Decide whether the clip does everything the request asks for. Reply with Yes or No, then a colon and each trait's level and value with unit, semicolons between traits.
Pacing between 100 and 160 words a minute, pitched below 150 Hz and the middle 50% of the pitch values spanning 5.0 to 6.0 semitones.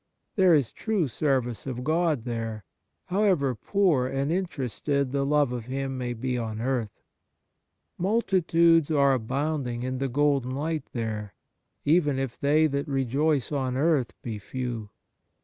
No: average, 140 wpm; low, 135 Hz; average, 4.0 semitones